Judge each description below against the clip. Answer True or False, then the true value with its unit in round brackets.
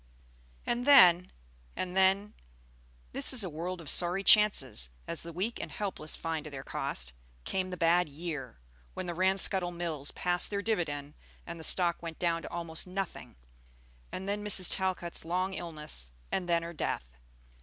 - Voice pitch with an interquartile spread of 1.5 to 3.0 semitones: True (2.7 semitones)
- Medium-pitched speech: True (175 Hz)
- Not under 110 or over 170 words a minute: True (165 wpm)